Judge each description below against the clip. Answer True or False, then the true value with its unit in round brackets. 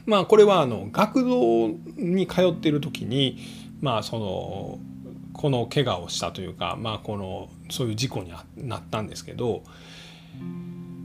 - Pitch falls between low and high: False (115 Hz)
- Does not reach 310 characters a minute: True (275 characters per minute)